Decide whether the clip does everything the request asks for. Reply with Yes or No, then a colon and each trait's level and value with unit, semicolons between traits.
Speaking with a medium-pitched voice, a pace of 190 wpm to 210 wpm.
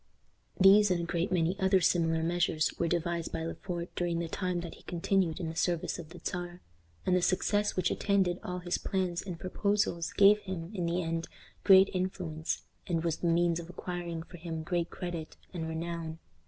Yes: medium, 175 Hz; average, 195 wpm